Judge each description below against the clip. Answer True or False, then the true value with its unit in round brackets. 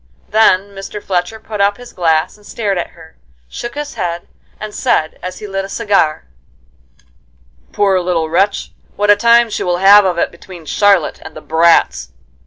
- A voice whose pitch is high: True (195 Hz)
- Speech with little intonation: False (3.2 semitones)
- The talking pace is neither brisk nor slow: True (180 wpm)